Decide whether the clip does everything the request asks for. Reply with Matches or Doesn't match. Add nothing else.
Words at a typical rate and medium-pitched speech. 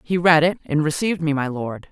Doesn't match